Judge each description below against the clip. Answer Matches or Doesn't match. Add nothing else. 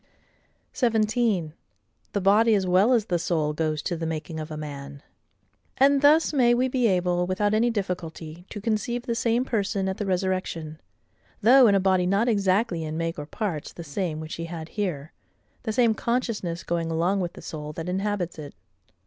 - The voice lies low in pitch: Doesn't match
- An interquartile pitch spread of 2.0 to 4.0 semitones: Doesn't match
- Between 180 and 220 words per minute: Matches